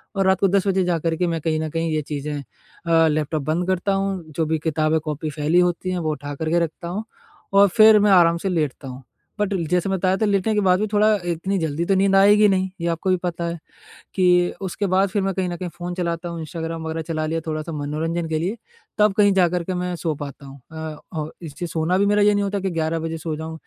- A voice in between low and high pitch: Yes, medium, 170 Hz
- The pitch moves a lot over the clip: No, average, 3.2 semitones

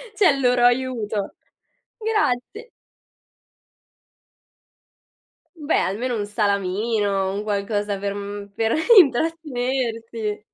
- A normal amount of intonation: Yes, average, 4.0 semitones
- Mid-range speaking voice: No, high, 225 Hz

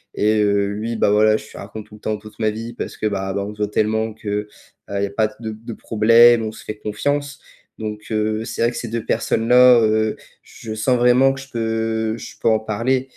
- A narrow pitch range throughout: Yes, narrow, 1.5 semitones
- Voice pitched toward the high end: No, low, 110 Hz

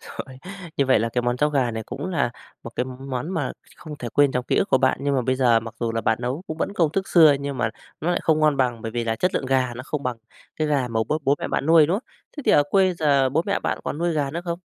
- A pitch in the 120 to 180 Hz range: Yes, low, 135 Hz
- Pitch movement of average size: Yes, average, 4.0 semitones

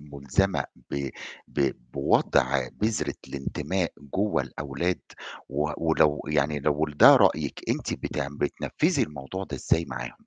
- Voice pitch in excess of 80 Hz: No, very low, 75 Hz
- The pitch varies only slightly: No, average, 3.3 semitones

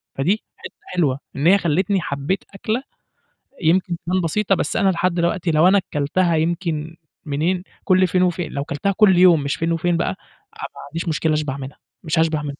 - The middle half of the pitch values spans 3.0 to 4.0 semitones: Yes, average, 3.3 semitones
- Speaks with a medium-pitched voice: Yes, medium, 170 Hz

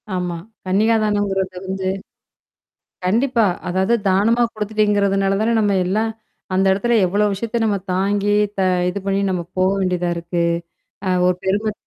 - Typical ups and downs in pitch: No, narrow, 2.3 semitones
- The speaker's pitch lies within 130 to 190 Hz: No, high, 200 Hz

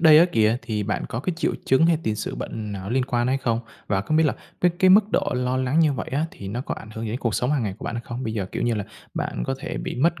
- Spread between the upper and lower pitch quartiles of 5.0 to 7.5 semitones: Yes, wide, 5.4 semitones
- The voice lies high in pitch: No, low, 125 Hz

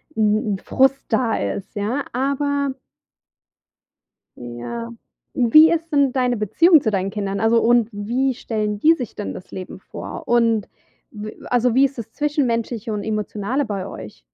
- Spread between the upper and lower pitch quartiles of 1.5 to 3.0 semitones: No, average, 4.2 semitones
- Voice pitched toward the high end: Yes, high, 230 Hz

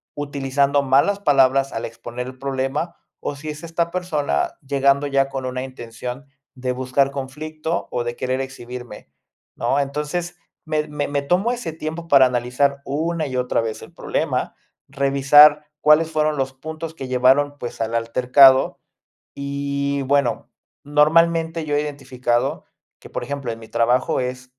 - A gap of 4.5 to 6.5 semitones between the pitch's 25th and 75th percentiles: No, average, 2.8 semitones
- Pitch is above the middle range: No, medium, 140 Hz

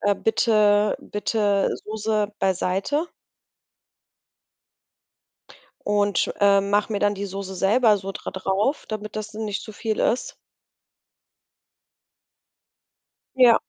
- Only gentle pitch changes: Yes, narrow, 1.6 semitones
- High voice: Yes, high, 205 Hz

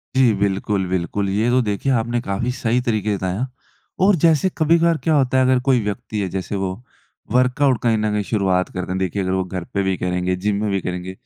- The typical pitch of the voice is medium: No, low, 105 Hz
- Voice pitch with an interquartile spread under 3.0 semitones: No, average, 4.9 semitones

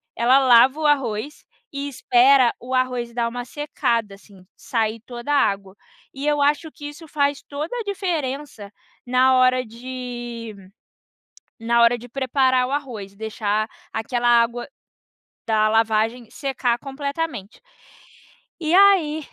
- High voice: Yes, very high, 250 Hz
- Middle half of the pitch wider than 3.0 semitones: Yes, average, 3.6 semitones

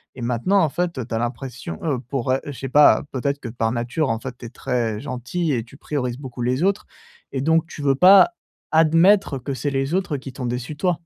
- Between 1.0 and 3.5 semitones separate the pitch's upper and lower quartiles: No, average, 4.2 semitones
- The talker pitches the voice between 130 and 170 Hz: Yes, low, 135 Hz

